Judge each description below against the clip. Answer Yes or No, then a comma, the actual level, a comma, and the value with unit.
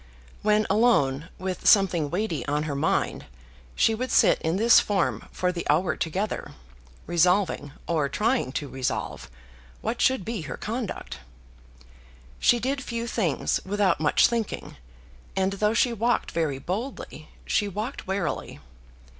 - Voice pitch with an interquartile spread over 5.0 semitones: Yes, wide, 5.6 semitones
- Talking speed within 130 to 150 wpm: Yes, average, 140 wpm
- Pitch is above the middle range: Yes, high, 195 Hz